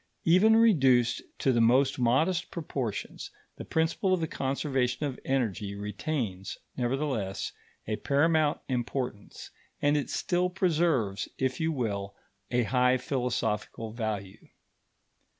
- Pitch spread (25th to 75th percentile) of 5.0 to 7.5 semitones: Yes, wide, 5.5 semitones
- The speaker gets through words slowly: Yes, slow, 115 wpm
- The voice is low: Yes, low, 130 Hz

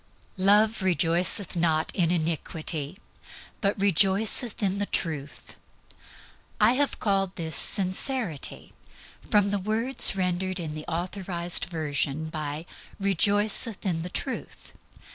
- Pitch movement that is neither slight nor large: Yes, average, 3.8 semitones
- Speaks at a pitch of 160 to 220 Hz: Yes, medium, 185 Hz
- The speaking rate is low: Yes, slow, 110 wpm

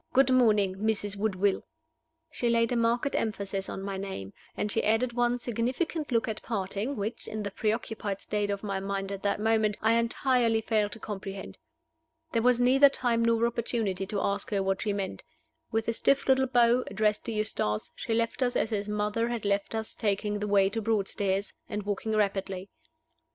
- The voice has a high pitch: Yes, high, 215 Hz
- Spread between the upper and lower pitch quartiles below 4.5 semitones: Yes, average, 2.7 semitones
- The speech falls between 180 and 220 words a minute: Yes, average, 190 wpm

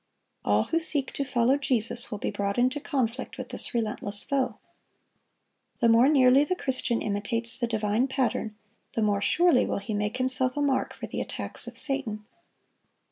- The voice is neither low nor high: No, high, 245 Hz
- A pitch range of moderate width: Yes, average, 4.0 semitones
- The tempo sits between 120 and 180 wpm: Yes, average, 175 wpm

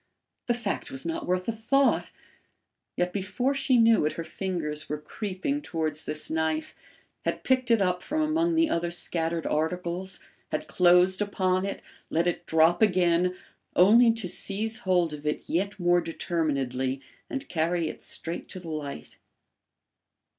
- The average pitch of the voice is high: No, medium, 180 Hz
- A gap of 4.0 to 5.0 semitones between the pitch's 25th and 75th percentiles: Yes, average, 4.6 semitones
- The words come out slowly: No, average, 155 wpm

